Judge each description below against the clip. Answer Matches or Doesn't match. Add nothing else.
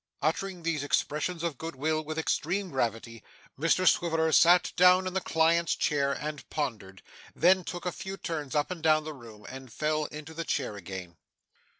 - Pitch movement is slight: Doesn't match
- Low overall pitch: Doesn't match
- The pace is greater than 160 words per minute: Matches